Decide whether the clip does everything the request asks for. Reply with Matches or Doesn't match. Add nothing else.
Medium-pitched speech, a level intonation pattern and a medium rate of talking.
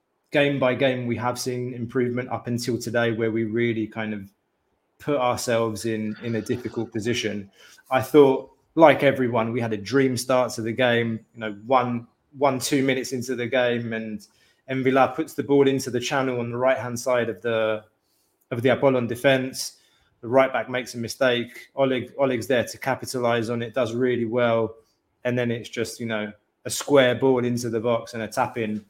Doesn't match